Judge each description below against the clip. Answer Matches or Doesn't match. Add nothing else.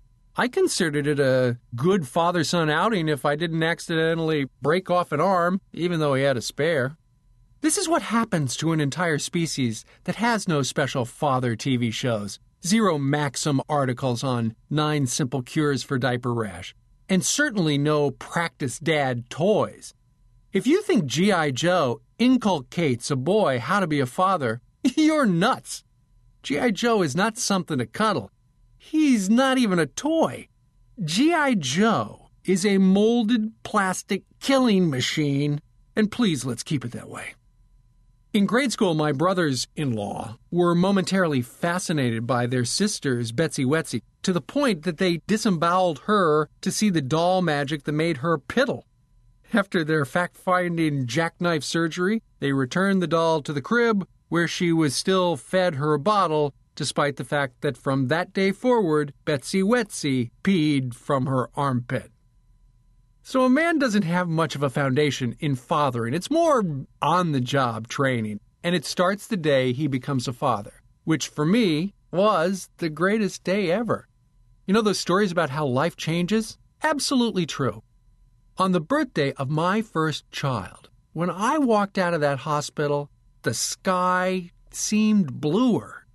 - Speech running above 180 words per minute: Doesn't match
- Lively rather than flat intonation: Matches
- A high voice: Doesn't match